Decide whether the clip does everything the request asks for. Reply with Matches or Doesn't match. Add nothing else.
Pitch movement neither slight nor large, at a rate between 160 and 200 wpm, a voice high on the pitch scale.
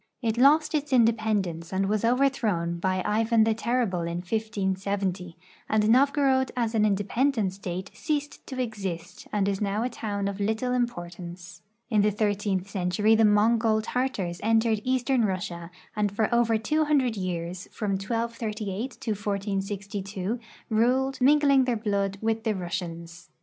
Doesn't match